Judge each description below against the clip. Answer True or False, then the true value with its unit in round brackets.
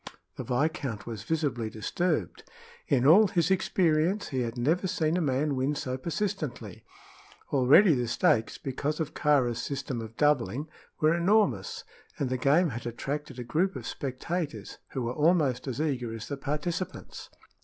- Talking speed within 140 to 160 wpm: True (155 wpm)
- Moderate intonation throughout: True (4.7 semitones)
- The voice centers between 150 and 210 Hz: False (140 Hz)